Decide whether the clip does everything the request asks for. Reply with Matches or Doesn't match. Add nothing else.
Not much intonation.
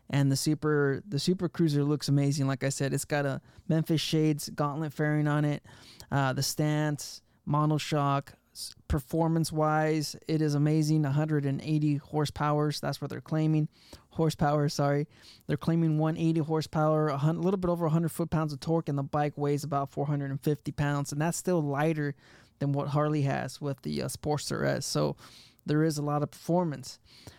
Matches